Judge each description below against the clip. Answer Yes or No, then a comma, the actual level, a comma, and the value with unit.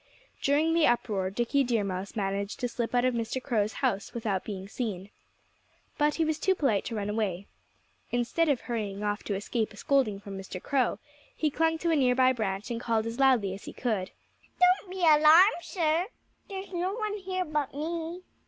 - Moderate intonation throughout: No, wide, 7.2 semitones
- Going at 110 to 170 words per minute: No, average, 195 wpm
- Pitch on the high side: Yes, high, 245 Hz